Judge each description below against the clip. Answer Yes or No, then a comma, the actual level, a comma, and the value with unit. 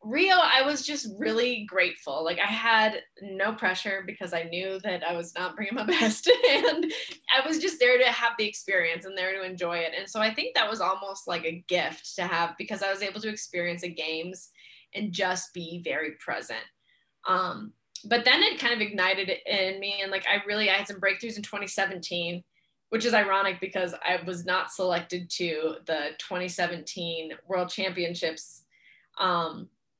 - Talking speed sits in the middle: Yes, average, 185 wpm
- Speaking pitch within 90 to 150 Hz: No, high, 190 Hz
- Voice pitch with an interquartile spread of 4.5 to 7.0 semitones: No, average, 3.4 semitones